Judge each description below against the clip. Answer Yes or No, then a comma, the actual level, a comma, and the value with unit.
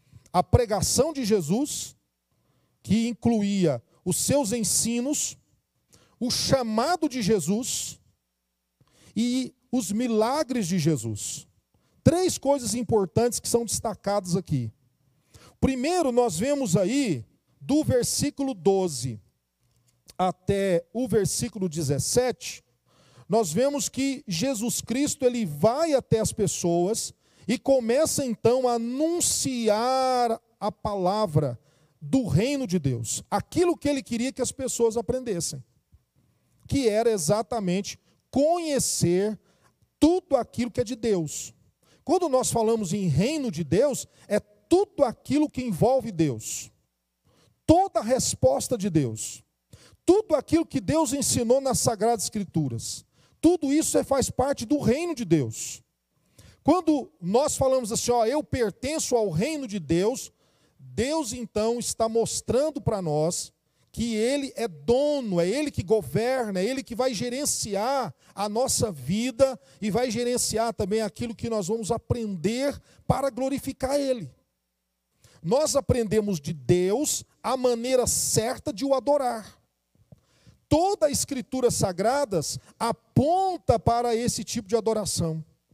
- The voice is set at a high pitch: Yes, high, 225 Hz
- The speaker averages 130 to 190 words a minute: No, slow, 120 wpm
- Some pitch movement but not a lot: No, wide, 7.2 semitones